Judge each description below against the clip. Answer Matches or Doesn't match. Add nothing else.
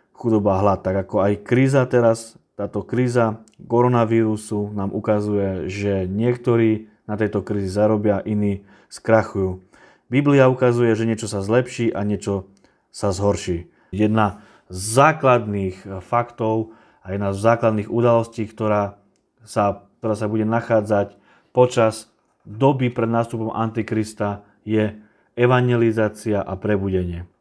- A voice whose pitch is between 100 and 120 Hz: Matches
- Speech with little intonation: Matches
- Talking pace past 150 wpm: Doesn't match